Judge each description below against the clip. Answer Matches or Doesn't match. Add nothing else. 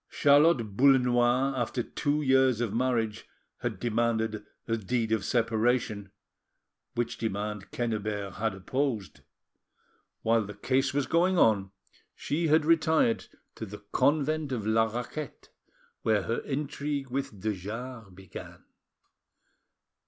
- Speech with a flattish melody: Doesn't match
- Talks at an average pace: Doesn't match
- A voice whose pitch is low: Matches